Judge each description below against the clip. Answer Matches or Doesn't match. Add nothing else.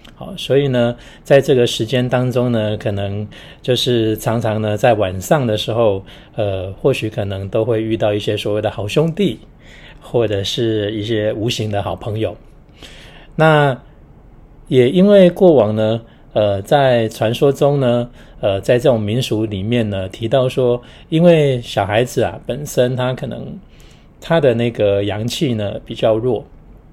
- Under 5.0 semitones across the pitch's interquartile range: Matches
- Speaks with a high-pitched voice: Doesn't match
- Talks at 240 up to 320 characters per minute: Doesn't match